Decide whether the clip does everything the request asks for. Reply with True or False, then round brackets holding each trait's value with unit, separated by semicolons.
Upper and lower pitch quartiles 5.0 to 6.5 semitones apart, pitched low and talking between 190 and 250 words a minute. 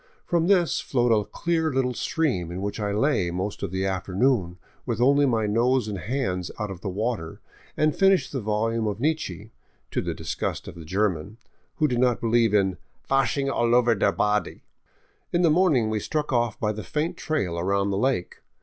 True (5.4 semitones; 115 Hz; 195 wpm)